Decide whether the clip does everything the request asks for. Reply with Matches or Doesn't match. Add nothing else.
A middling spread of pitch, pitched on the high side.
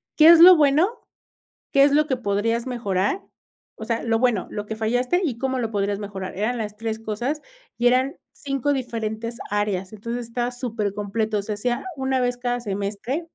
Matches